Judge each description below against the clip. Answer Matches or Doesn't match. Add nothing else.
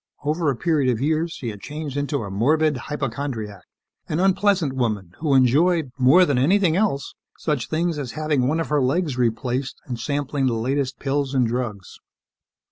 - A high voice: Doesn't match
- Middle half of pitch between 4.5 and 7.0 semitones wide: Doesn't match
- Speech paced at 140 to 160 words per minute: Doesn't match